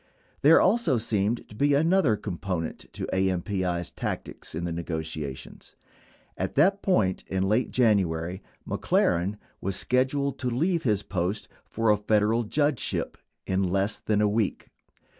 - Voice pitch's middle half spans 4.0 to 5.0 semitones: No, wide, 5.5 semitones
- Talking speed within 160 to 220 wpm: No, average, 140 wpm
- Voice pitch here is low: Yes, low, 105 Hz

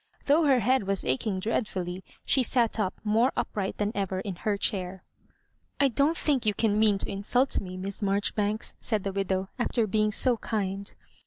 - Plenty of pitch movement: No, average, 3.1 semitones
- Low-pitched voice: No, high, 205 Hz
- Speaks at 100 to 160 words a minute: No, average, 185 wpm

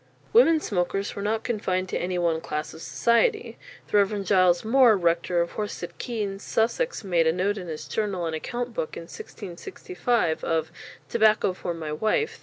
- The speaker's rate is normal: Yes, average, 180 wpm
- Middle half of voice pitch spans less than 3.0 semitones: No, average, 4.6 semitones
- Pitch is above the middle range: Yes, high, 195 Hz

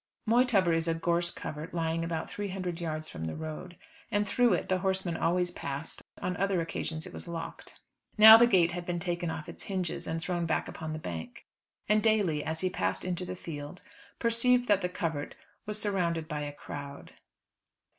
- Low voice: No, medium, 175 Hz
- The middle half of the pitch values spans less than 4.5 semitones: Yes, average, 3.0 semitones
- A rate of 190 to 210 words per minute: Yes, average, 195 wpm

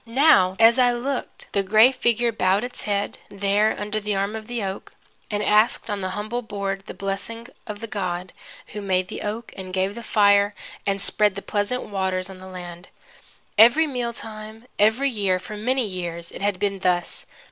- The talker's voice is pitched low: No, high, 205 Hz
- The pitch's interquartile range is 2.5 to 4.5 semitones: Yes, average, 2.9 semitones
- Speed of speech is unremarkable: Yes, average, 190 wpm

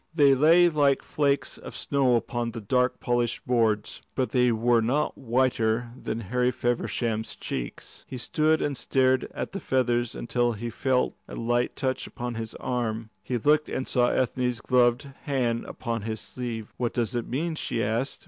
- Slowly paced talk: No, average, 170 wpm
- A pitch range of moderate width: No, narrow, 2.2 semitones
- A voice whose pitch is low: Yes, low, 120 Hz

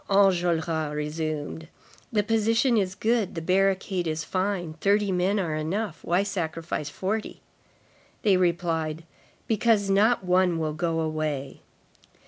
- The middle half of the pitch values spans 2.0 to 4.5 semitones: Yes, average, 3.9 semitones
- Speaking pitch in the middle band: Yes, medium, 180 Hz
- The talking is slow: Yes, slow, 120 wpm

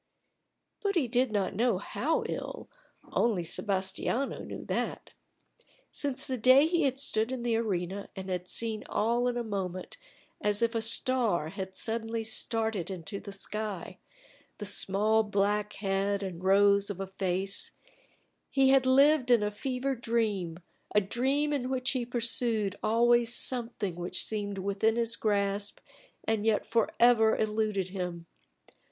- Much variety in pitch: No, average, 3.4 semitones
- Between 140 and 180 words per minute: Yes, average, 150 wpm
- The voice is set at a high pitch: Yes, high, 220 Hz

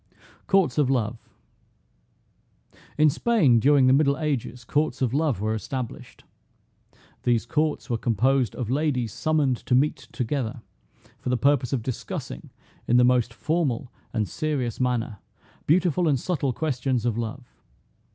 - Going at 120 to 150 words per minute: Yes, average, 140 wpm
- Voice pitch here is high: No, low, 130 Hz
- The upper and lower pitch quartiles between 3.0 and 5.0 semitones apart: Yes, average, 3.7 semitones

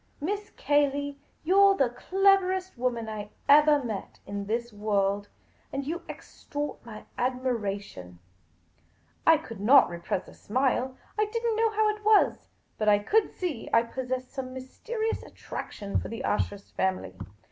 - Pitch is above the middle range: Yes, very high, 255 Hz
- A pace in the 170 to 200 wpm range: No, average, 155 wpm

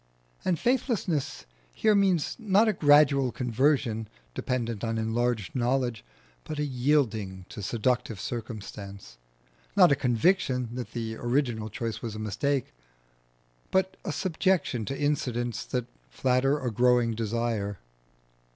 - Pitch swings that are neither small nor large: Yes, average, 4.5 semitones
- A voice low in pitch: Yes, low, 125 Hz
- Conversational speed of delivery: No, slow, 125 wpm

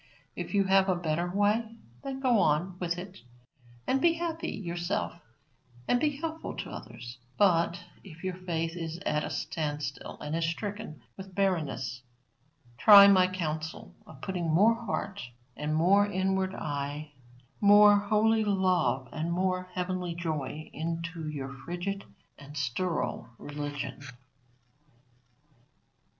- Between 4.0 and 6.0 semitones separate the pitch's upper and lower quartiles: Yes, average, 4.3 semitones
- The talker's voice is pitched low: No, medium, 180 Hz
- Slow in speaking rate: Yes, slow, 130 wpm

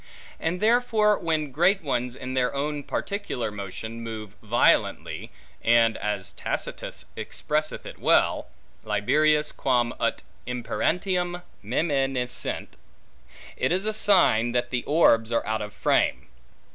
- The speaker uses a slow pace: Yes, slow, 120 wpm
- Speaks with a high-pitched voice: No, low, 130 Hz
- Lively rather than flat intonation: Yes, wide, 6.8 semitones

